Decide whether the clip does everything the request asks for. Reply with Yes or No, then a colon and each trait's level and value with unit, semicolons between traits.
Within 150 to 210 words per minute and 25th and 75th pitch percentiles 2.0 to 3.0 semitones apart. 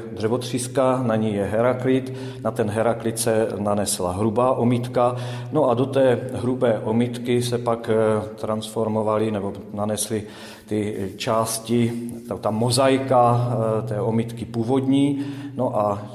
No: average, 125 wpm; narrow, 2.3 semitones